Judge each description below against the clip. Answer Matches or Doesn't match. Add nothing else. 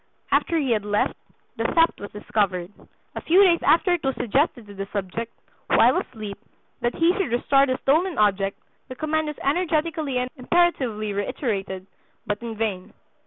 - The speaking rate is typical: Matches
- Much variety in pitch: Matches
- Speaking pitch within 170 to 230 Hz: Doesn't match